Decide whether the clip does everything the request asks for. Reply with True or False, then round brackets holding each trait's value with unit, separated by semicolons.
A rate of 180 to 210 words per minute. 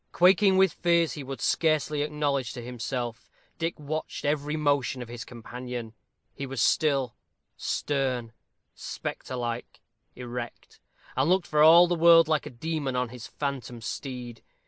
False (145 wpm)